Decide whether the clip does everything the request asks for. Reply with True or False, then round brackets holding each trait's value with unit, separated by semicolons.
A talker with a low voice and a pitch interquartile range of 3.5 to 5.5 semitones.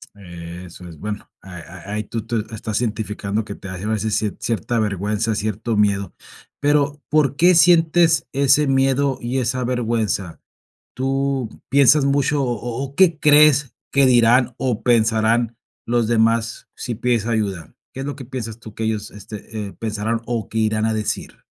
True (115 Hz; 4.1 semitones)